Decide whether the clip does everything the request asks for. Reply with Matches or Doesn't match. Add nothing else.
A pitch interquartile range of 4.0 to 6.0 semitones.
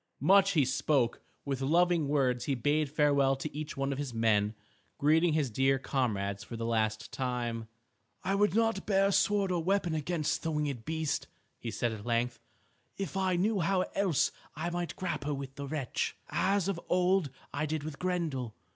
Matches